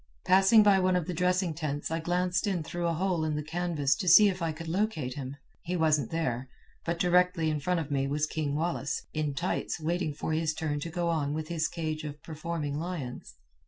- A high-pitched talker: No, medium, 160 Hz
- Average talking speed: No, fast, 220 wpm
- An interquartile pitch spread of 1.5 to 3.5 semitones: Yes, average, 2.9 semitones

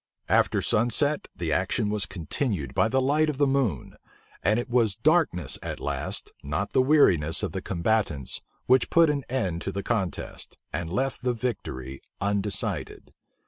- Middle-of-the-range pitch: No, low, 105 Hz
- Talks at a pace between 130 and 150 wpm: No, average, 160 wpm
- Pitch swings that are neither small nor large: No, wide, 7.1 semitones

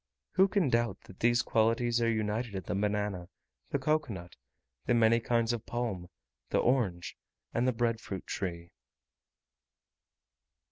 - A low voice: Yes, low, 115 Hz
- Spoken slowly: No, average, 145 wpm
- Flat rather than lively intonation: No, average, 3.1 semitones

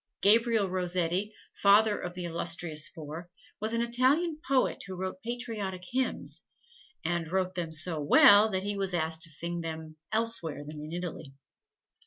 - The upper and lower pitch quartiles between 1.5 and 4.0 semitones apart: No, average, 4.8 semitones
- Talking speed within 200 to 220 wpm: No, average, 155 wpm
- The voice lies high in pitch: No, medium, 180 Hz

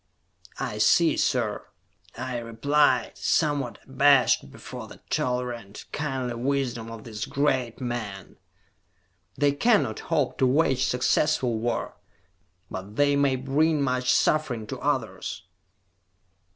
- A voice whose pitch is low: Yes, low, 130 Hz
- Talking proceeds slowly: Yes, slow, 110 wpm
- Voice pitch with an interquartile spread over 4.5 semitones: No, average, 3.4 semitones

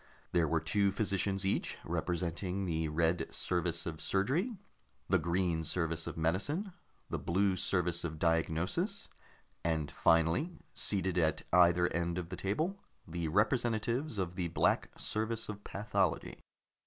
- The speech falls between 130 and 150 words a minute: Yes, slow, 135 wpm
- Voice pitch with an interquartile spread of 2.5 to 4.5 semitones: Yes, average, 3.7 semitones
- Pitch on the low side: Yes, very low, 90 Hz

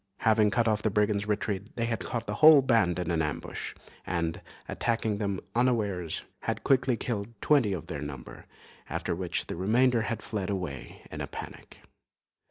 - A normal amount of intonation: Yes, average, 4.3 semitones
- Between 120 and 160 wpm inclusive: No, average, 175 wpm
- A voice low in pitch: Yes, low, 105 Hz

